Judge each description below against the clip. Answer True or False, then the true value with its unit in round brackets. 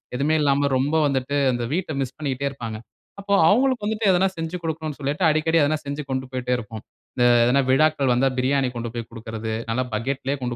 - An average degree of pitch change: True (3.9 semitones)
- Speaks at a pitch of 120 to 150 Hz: True (140 Hz)